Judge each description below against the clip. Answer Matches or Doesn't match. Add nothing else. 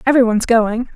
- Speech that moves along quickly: Doesn't match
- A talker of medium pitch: Doesn't match